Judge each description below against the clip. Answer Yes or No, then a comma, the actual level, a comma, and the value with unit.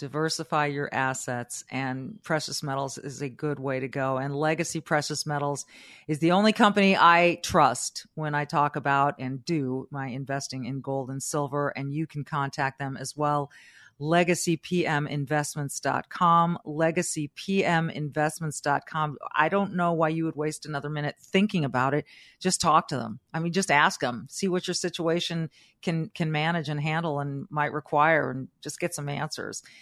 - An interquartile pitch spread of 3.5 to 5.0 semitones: No, average, 2.9 semitones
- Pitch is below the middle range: No, medium, 150 Hz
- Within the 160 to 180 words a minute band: Yes, average, 165 wpm